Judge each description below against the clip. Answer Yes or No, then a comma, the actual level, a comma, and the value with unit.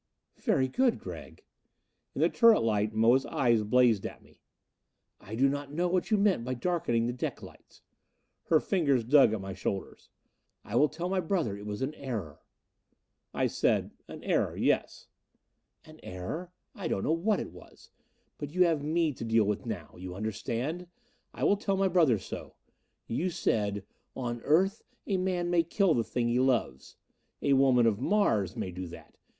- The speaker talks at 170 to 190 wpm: Yes, average, 180 wpm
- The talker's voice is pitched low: Yes, low, 130 Hz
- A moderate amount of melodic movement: No, wide, 7.8 semitones